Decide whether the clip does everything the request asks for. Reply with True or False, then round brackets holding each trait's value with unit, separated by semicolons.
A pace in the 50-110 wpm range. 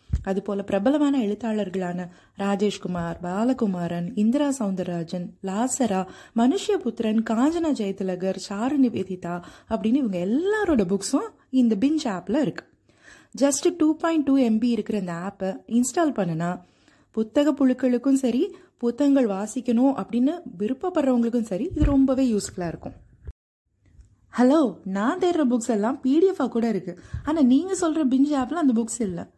False (120 wpm)